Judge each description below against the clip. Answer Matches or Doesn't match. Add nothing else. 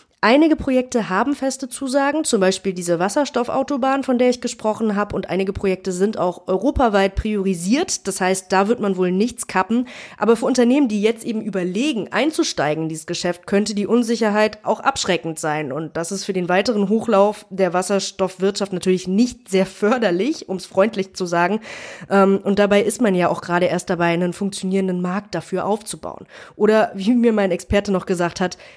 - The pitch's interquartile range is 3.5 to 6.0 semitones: Matches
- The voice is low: Doesn't match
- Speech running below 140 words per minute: Doesn't match